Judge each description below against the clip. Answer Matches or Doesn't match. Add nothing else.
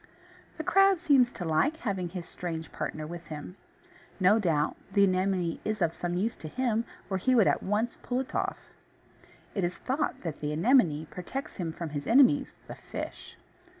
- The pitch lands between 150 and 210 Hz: Matches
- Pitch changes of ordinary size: Doesn't match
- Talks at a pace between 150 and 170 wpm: Doesn't match